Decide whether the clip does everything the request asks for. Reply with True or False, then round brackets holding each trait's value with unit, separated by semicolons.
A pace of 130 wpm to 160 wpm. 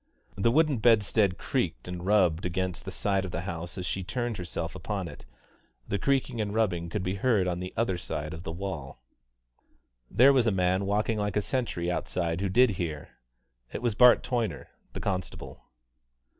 False (185 wpm)